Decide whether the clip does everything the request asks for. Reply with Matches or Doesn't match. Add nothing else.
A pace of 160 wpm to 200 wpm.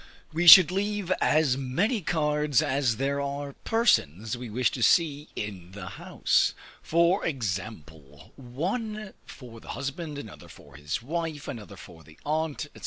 Doesn't match